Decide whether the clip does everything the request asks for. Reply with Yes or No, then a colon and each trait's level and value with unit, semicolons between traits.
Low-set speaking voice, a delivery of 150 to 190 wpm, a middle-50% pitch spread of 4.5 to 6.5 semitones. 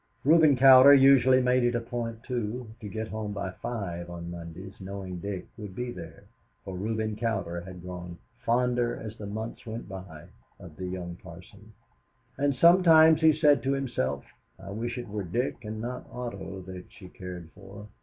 Yes: low, 110 Hz; average, 175 wpm; average, 5.0 semitones